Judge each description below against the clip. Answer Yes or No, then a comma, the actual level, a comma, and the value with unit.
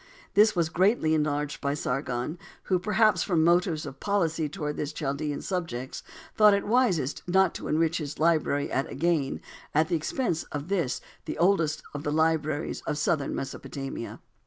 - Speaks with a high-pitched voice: No, medium, 160 Hz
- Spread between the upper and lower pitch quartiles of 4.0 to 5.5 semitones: No, average, 3.5 semitones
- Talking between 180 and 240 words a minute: No, average, 160 wpm